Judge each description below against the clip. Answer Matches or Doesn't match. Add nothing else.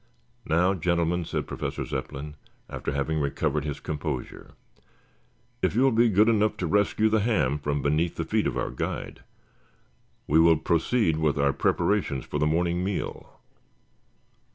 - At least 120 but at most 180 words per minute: Matches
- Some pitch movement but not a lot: Matches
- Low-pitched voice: Matches